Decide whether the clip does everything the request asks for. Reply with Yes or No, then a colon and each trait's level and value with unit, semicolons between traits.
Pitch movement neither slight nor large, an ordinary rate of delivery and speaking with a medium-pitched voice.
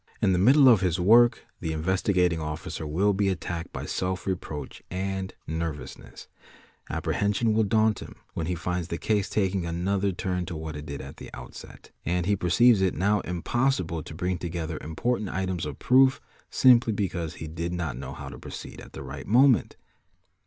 No: average, 3.7 semitones; average, 180 wpm; very low, 90 Hz